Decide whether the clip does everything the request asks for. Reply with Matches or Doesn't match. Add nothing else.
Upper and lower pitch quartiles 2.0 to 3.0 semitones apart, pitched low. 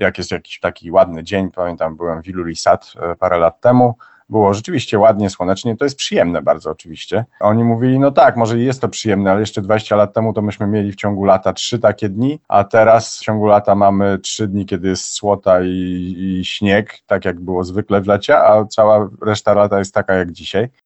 Matches